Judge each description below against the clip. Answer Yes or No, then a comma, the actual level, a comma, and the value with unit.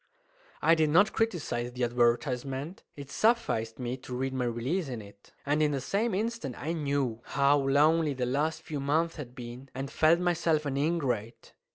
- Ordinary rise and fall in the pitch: Yes, average, 4.4 semitones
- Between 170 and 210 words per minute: Yes, average, 180 wpm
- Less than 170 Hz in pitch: Yes, medium, 140 Hz